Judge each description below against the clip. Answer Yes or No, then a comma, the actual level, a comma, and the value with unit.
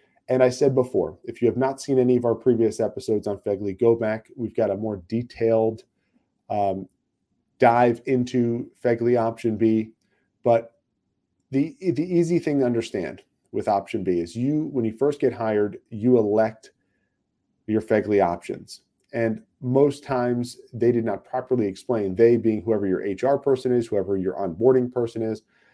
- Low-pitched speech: Yes, low, 115 Hz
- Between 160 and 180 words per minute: Yes, average, 165 wpm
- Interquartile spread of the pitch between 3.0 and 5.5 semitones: No, narrow, 2.6 semitones